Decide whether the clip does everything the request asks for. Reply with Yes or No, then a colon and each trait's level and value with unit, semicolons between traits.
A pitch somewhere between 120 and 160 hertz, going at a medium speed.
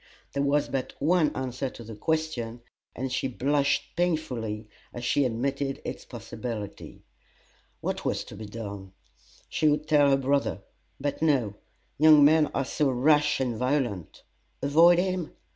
Yes: medium, 140 Hz; average, 145 wpm